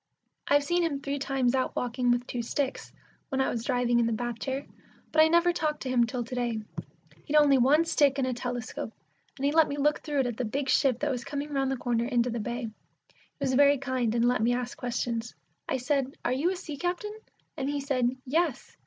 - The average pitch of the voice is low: No, very high, 265 Hz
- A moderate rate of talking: No, fast, 235 wpm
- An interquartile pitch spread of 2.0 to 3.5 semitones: Yes, average, 2.9 semitones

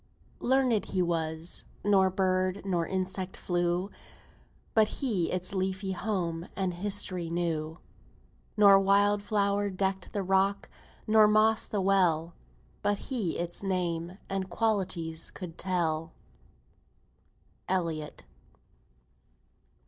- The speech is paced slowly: Yes, slow, 105 wpm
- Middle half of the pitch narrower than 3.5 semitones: Yes, narrow, 2.6 semitones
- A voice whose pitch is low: No, high, 190 Hz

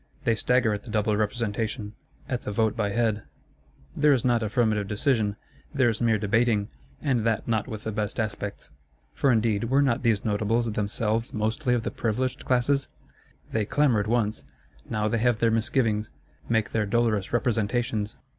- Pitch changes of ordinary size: No, narrow, 2.2 semitones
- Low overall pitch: Yes, low, 110 Hz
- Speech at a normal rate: Yes, average, 165 wpm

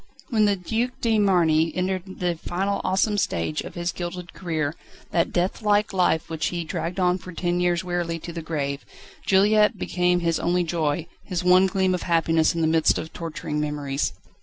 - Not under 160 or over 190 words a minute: Yes, average, 185 wpm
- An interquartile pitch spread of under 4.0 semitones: Yes, narrow, 2.5 semitones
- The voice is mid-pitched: Yes, medium, 175 Hz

